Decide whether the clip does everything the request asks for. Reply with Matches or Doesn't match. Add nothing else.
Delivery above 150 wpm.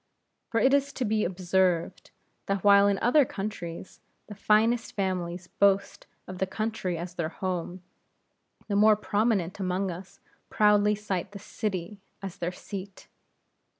Doesn't match